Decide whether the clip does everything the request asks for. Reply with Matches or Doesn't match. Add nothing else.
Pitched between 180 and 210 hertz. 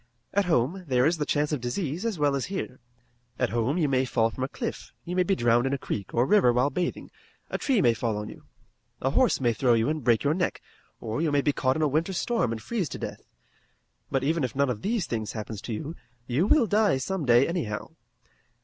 Doesn't match